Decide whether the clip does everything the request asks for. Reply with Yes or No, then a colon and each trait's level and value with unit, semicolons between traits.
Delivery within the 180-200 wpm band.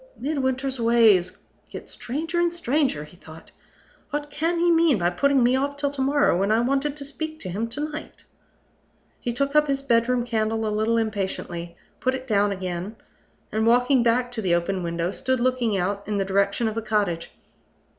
Yes: average, 190 wpm